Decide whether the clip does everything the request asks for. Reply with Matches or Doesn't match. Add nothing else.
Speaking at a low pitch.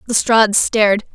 Doesn't match